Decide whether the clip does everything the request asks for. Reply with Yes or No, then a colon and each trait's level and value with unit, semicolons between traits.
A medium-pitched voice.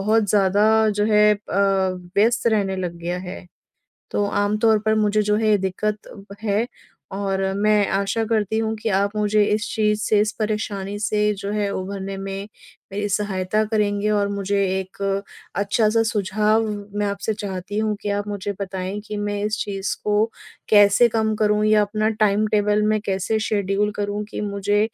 No: high, 205 Hz